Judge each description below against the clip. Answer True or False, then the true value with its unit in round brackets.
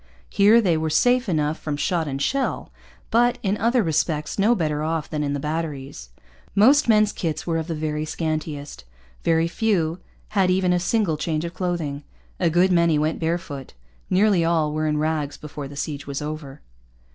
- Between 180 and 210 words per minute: True (185 wpm)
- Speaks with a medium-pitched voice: True (160 Hz)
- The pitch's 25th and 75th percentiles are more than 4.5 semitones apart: False (3.6 semitones)